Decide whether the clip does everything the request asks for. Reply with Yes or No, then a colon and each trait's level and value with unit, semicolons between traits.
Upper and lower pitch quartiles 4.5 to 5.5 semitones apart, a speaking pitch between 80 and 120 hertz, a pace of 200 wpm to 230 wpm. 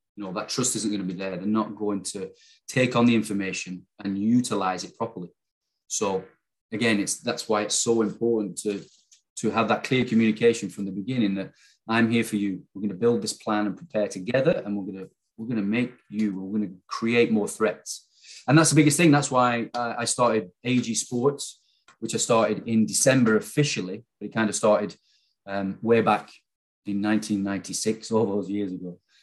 No: average, 2.9 semitones; low, 110 Hz; fast, 205 wpm